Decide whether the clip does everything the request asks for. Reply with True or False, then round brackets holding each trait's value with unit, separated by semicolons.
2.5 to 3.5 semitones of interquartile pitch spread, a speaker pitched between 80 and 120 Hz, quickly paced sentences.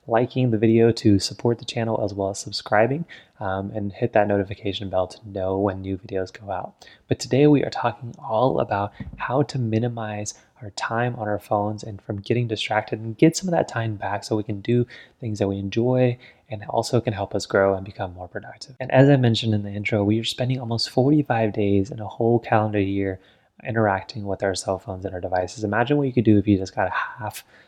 True (3.1 semitones; 110 Hz; 230 wpm)